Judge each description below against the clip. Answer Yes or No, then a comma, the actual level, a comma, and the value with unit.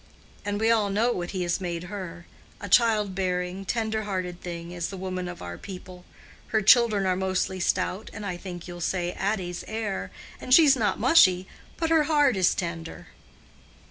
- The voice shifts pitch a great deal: No, average, 3.4 semitones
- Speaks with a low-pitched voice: No, high, 190 Hz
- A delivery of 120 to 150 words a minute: No, average, 175 wpm